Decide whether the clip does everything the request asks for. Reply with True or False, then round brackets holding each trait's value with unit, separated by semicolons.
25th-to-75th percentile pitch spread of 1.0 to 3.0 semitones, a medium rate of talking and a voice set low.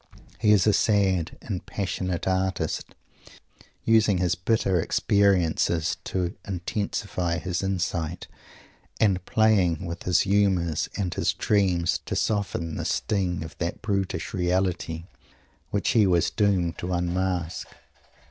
False (2.5 semitones; 120 wpm; 90 Hz)